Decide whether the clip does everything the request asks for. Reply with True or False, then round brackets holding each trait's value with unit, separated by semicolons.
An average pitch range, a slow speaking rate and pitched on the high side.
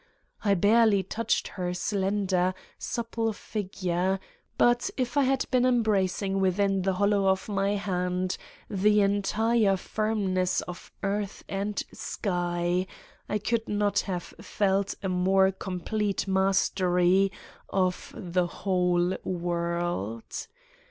False (2.3 semitones; 110 wpm; 195 Hz)